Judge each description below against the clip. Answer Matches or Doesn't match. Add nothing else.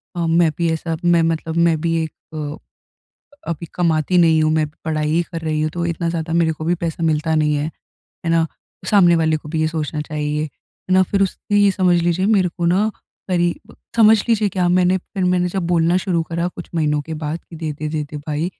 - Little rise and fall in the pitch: Matches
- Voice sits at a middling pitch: Matches